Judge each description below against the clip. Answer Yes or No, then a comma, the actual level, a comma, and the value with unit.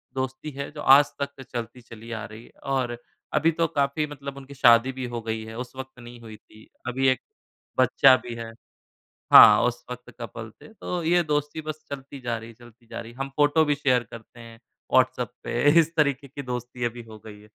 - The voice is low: Yes, low, 125 Hz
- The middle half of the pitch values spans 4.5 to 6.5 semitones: No, average, 3.3 semitones